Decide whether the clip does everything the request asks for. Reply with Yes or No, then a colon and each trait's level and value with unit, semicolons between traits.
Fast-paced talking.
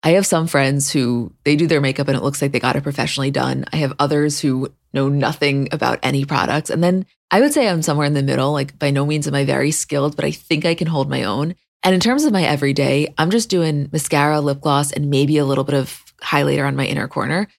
Yes: fast, 260 wpm